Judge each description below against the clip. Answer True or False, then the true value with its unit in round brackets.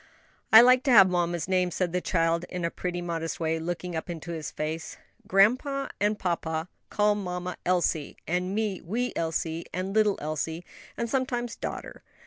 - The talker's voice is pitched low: False (180 Hz)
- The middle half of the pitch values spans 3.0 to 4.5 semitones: True (3.9 semitones)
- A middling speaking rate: True (170 wpm)